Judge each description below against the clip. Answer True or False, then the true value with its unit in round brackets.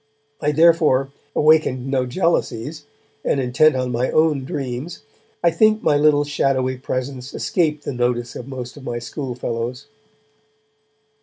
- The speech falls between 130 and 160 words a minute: True (135 wpm)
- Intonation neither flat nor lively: True (3.4 semitones)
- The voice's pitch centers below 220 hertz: True (135 Hz)